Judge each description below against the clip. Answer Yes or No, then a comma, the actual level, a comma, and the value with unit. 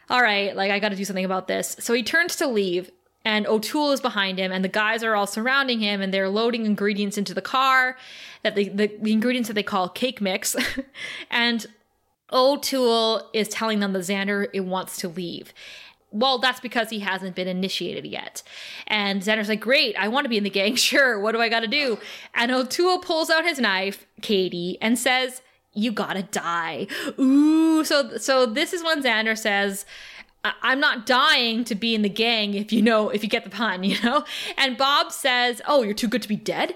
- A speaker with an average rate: No, fast, 210 wpm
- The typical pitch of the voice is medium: No, high, 225 Hz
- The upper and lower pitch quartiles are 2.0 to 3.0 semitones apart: No, average, 4.3 semitones